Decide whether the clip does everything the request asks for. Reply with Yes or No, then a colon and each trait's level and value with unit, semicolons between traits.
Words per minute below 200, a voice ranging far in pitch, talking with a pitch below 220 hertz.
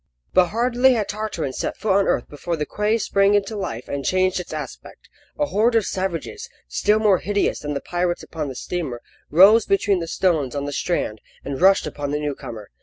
No: fast, 205 wpm; wide, 6.0 semitones; medium, 185 Hz